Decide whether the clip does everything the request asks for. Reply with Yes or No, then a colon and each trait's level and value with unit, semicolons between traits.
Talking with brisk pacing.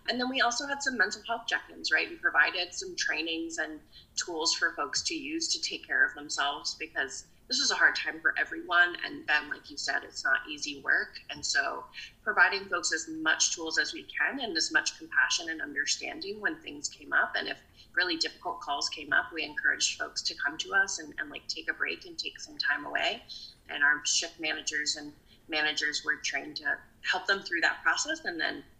Yes: fast, 215 wpm